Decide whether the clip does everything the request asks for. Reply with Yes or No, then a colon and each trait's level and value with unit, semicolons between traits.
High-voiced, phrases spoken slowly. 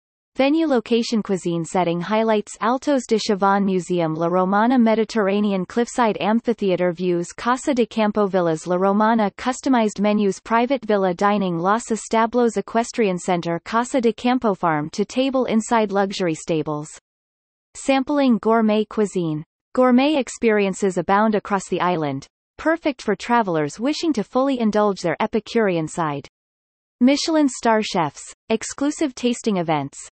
Yes: high, 210 Hz; slow, 125 wpm